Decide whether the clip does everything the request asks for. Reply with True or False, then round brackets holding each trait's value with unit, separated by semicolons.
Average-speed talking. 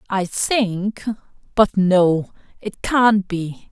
False (95 wpm)